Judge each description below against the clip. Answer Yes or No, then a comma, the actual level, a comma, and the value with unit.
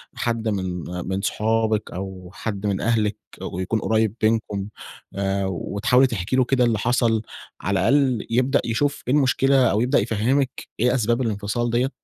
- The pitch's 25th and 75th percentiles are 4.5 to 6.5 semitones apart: No, average, 3.8 semitones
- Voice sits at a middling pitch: No, low, 110 Hz